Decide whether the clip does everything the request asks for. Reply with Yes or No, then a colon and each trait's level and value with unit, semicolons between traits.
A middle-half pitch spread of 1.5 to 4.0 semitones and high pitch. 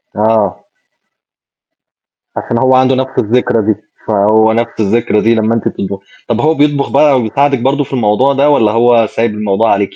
No: average, 3.5 semitones; low, 115 Hz